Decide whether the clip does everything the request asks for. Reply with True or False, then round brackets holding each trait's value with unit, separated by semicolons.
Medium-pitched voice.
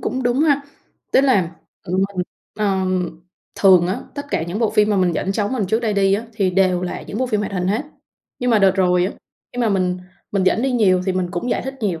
False (195 Hz)